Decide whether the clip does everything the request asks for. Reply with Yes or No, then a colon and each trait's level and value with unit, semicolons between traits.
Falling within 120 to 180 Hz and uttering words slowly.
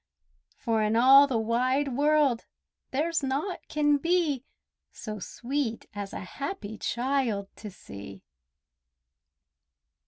No: very high, 260 Hz; slow, 105 wpm